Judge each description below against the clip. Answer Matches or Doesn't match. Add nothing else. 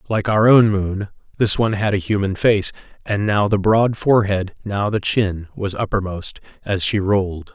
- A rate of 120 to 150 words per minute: Doesn't match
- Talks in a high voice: Doesn't match